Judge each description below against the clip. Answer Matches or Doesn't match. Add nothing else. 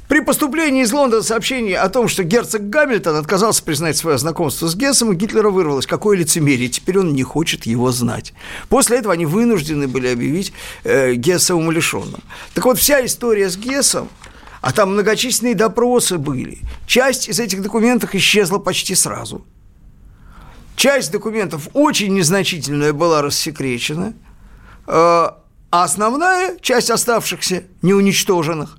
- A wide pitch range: Matches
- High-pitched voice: Matches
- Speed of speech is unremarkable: Matches